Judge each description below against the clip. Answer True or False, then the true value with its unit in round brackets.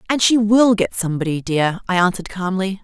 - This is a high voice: True (195 Hz)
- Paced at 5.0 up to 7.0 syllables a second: True (5.9 syllables/s)